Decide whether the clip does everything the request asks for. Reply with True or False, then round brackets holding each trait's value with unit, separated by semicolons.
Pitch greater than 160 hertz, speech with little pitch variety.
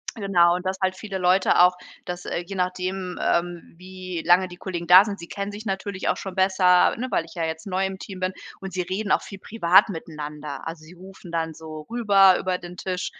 True (185 Hz; 1.9 semitones)